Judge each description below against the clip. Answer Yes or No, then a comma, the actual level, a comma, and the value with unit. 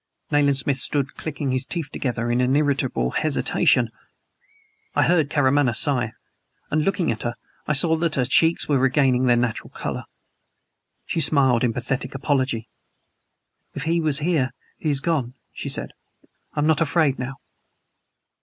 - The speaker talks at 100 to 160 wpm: Yes, average, 155 wpm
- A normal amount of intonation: Yes, average, 3.2 semitones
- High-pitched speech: No, medium, 140 Hz